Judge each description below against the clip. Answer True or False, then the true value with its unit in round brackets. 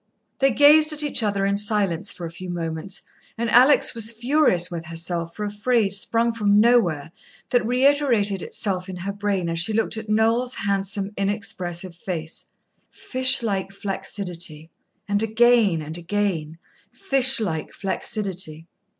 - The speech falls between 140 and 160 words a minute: True (150 wpm)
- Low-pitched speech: False (200 Hz)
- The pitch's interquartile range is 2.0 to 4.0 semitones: False (4.6 semitones)